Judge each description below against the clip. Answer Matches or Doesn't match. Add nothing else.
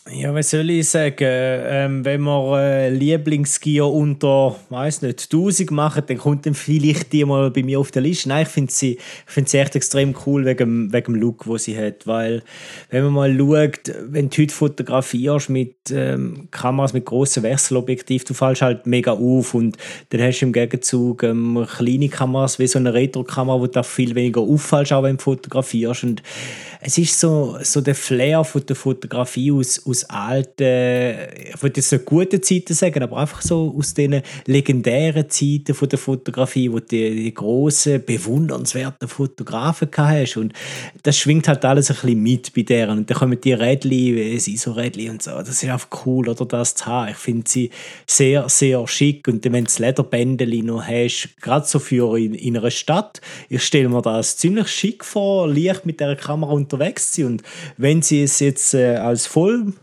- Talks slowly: Doesn't match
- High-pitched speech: Doesn't match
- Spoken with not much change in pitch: Doesn't match